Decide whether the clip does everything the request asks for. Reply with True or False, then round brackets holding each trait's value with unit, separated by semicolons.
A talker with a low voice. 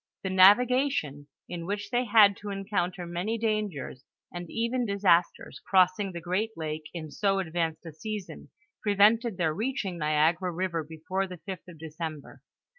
False (185 Hz)